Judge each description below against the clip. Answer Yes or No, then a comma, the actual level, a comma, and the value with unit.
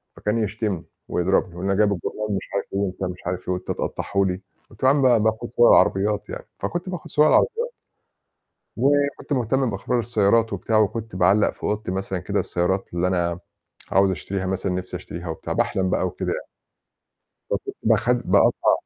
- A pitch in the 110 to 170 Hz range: No, low, 100 Hz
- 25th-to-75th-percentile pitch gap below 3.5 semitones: No, average, 3.9 semitones